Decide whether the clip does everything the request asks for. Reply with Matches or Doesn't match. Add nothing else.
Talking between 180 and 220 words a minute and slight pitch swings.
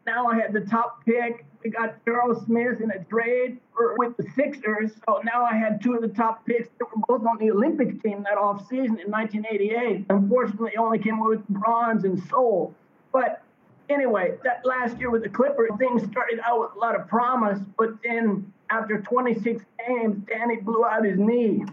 Matches